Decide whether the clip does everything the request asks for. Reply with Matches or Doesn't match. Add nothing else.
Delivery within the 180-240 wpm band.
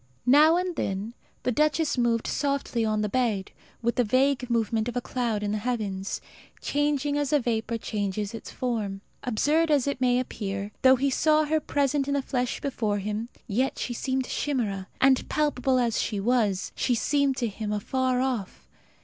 Matches